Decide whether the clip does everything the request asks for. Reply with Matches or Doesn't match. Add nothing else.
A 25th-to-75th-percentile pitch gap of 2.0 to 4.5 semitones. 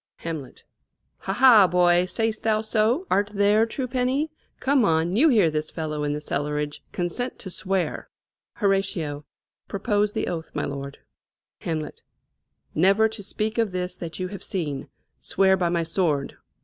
Doesn't match